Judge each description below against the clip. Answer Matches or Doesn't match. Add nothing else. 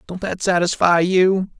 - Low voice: Doesn't match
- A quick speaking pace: Doesn't match